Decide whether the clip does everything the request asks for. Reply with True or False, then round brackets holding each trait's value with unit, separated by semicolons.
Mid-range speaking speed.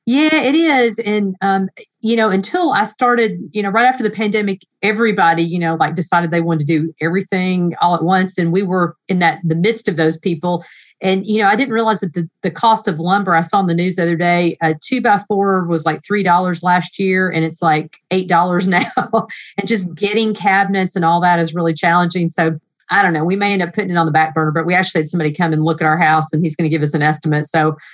False (250 wpm)